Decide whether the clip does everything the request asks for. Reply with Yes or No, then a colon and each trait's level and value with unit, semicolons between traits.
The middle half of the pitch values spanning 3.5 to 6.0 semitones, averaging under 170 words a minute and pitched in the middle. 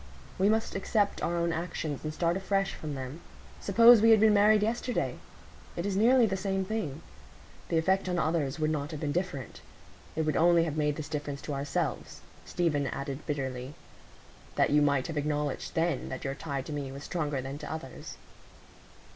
No: average, 5.0 semitones; average, 190 wpm; medium, 160 Hz